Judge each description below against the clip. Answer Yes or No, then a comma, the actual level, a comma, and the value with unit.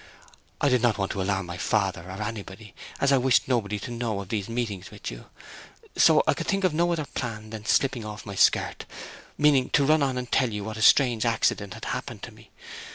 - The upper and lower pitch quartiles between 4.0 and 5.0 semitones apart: Yes, average, 4.4 semitones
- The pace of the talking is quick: Yes, fast, 225 wpm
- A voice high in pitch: No, low, 110 Hz